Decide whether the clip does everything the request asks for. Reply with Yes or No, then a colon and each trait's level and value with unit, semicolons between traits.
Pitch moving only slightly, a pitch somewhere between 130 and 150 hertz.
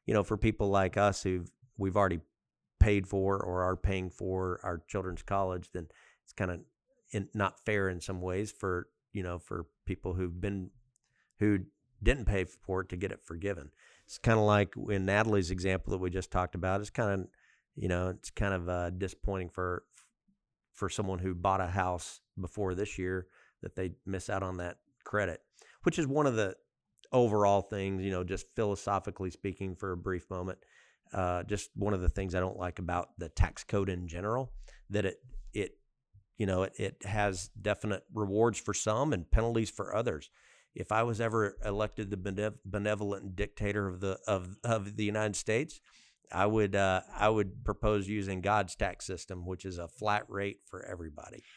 No: narrow, 2.2 semitones; low, 100 Hz